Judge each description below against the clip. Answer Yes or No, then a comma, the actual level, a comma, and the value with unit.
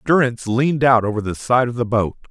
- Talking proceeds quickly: Yes, fast, 235 wpm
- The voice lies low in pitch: Yes, low, 120 Hz